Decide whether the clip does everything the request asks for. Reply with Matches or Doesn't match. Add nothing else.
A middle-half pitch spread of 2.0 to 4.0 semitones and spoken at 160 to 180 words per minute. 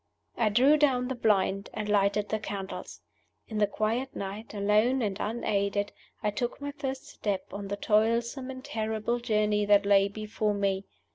Matches